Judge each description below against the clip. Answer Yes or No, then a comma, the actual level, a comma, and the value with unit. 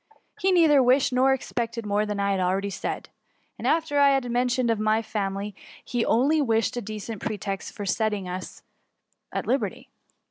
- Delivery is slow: No, average, 180 wpm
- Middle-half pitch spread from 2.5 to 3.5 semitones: No, average, 4.2 semitones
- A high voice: Yes, high, 225 Hz